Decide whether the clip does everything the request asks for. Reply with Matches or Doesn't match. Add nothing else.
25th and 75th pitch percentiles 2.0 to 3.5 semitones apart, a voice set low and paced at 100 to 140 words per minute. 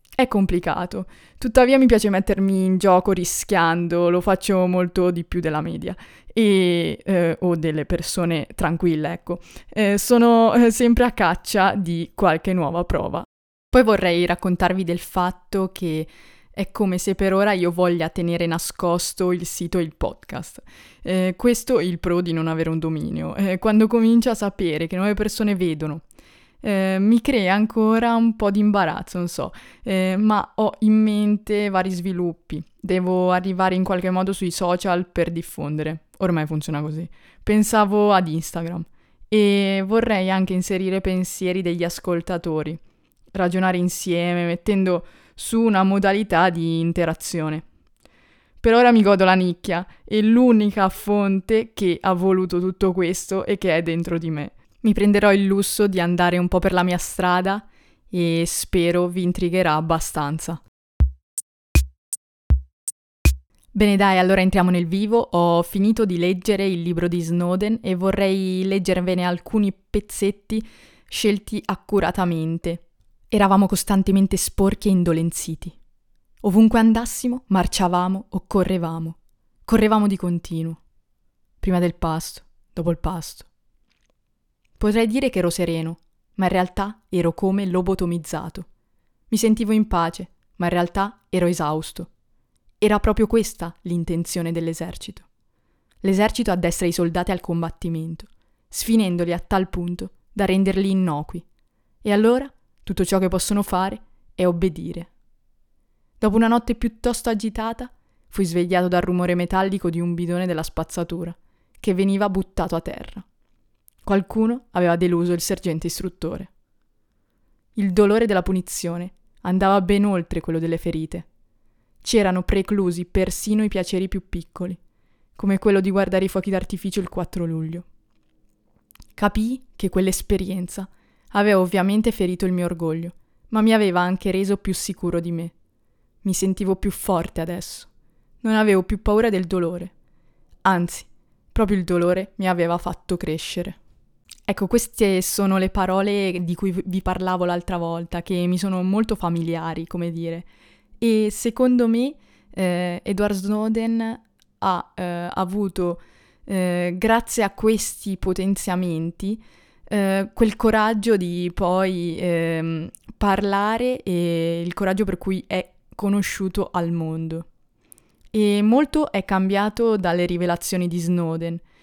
Doesn't match